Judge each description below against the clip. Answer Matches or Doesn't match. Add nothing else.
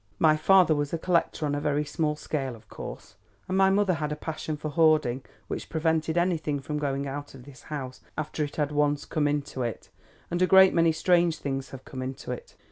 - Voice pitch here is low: Doesn't match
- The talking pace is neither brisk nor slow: Doesn't match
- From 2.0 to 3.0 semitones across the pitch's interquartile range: Matches